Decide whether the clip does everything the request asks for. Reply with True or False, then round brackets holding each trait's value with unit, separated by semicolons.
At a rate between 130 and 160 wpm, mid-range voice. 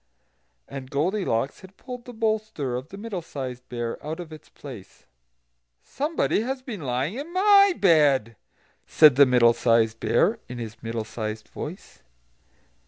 True (150 wpm; 145 Hz)